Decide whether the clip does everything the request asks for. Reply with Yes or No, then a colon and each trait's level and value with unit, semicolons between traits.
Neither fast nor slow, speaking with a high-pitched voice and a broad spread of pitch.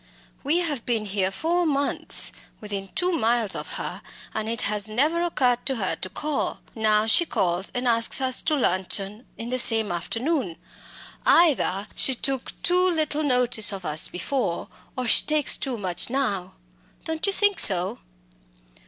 Yes: average, 160 wpm; high, 240 Hz; wide, 6.6 semitones